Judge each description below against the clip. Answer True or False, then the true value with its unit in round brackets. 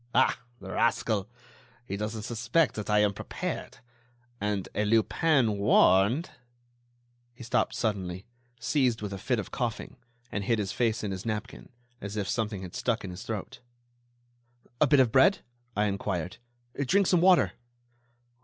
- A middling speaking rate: True (155 wpm)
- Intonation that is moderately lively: True (3.5 semitones)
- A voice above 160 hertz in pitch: False (110 Hz)